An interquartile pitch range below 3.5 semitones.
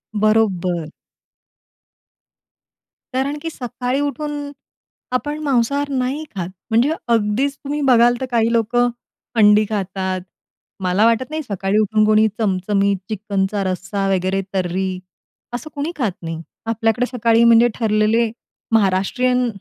No: average, 4.3 semitones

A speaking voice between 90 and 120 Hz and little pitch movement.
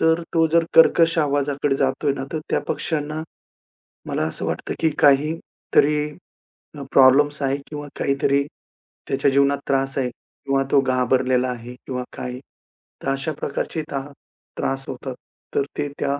No: medium, 140 Hz; narrow, 1.8 semitones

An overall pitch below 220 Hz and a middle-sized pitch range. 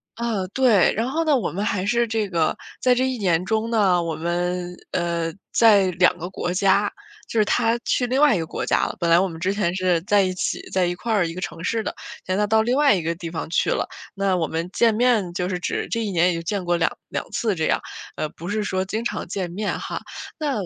Yes: high, 190 Hz; average, 4.2 semitones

